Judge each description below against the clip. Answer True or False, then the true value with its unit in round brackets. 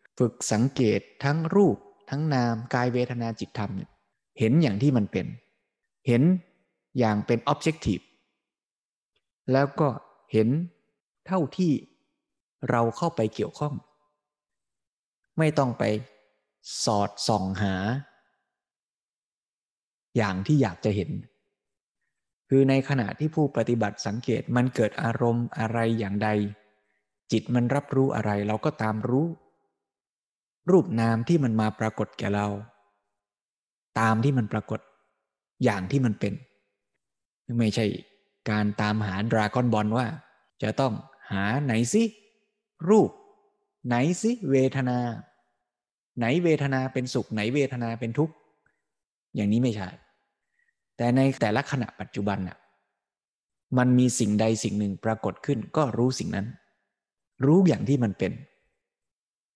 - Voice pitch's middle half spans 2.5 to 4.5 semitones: False (4.9 semitones)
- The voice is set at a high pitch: False (120 Hz)